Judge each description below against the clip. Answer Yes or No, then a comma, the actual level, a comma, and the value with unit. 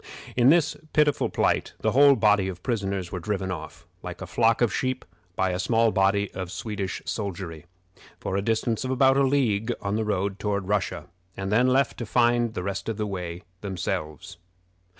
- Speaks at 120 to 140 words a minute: No, average, 190 wpm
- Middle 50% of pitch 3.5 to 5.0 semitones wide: Yes, average, 4.1 semitones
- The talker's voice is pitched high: No, low, 100 Hz